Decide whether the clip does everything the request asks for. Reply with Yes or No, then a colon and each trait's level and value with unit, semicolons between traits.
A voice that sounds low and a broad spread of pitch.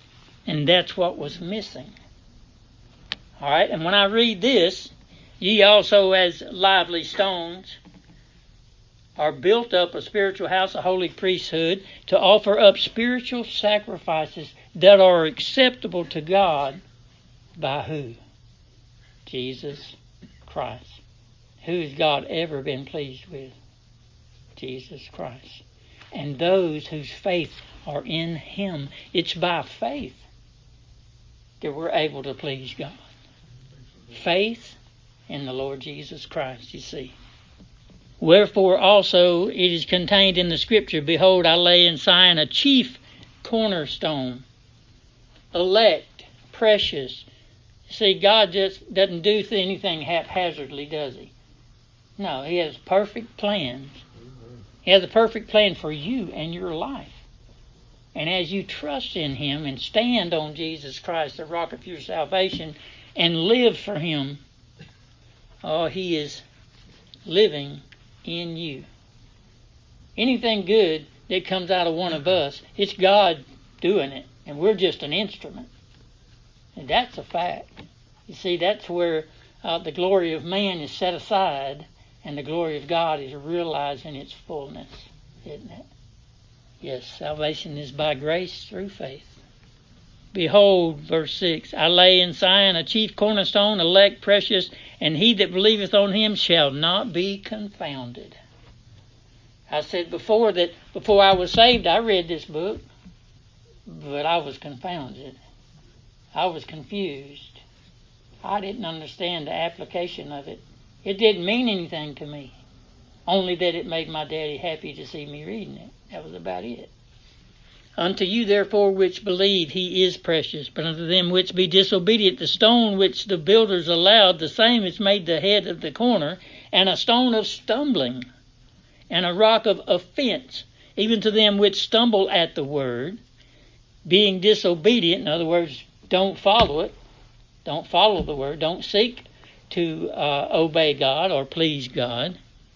No: medium, 165 Hz; wide, 6.2 semitones